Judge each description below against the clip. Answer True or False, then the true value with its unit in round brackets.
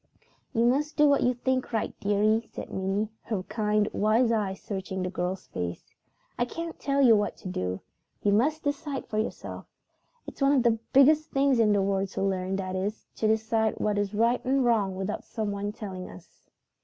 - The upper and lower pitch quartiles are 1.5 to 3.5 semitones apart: False (4.3 semitones)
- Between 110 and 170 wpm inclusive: False (190 wpm)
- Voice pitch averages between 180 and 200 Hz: False (215 Hz)